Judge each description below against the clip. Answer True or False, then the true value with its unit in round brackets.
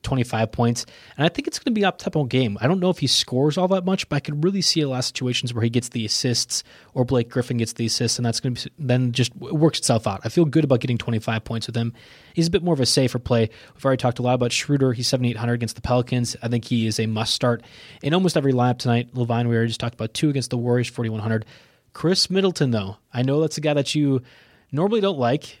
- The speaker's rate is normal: False (275 wpm)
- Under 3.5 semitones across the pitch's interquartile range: False (4.1 semitones)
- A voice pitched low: True (125 Hz)